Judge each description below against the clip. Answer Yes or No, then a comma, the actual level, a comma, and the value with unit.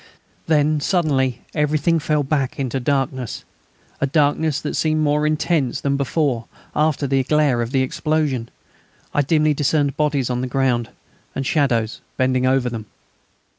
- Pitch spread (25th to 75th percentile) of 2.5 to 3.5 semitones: Yes, average, 2.8 semitones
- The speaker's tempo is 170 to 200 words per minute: No, average, 145 wpm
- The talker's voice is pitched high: No, medium, 140 Hz